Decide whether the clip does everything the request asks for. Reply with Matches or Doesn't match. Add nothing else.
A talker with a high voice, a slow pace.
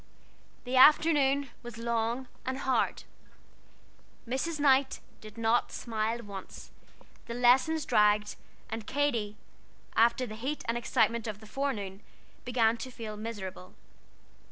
Matches